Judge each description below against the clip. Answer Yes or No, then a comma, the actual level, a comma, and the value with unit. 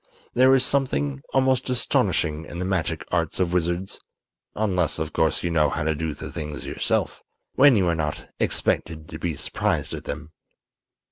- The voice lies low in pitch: Yes, very low, 85 Hz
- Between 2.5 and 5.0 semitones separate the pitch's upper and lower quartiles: Yes, average, 3.8 semitones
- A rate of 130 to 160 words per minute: No, average, 175 wpm